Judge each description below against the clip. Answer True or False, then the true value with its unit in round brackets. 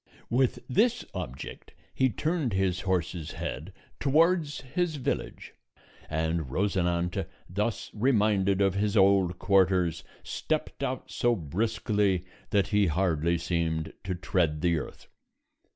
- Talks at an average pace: False (120 wpm)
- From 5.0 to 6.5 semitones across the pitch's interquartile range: False (4.5 semitones)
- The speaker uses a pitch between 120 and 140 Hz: False (95 Hz)